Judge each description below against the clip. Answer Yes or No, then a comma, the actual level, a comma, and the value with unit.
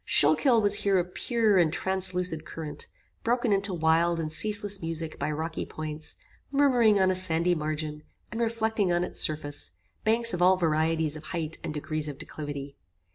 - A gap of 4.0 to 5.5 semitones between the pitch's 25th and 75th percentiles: Yes, average, 4.6 semitones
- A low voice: No, medium, 175 Hz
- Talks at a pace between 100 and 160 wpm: No, average, 170 wpm